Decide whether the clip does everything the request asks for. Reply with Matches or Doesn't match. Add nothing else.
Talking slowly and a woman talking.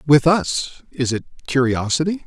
Doesn't match